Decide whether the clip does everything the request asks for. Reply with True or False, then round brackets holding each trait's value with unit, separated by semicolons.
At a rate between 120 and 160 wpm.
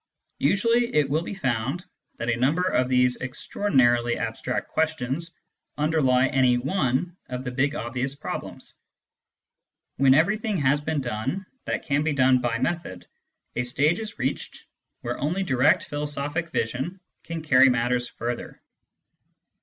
True (140 wpm)